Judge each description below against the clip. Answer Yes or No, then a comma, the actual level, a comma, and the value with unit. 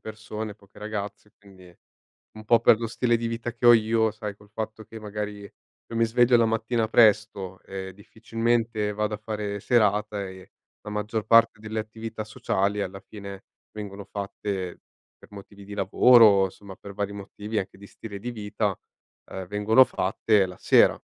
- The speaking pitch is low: Yes, low, 105 Hz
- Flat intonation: Yes, narrow, 1.9 semitones